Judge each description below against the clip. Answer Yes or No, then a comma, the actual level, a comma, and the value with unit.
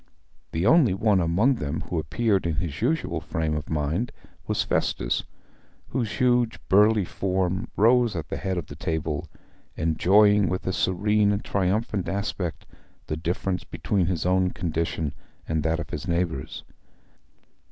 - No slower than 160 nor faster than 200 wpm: No, average, 150 wpm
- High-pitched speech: No, very low, 95 Hz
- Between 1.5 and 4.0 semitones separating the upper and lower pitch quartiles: No, average, 4.4 semitones